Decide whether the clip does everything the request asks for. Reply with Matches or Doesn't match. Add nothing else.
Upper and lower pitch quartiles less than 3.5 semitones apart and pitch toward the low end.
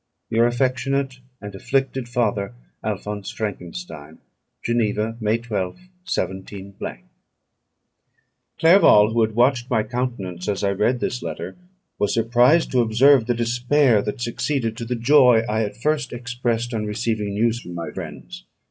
Matches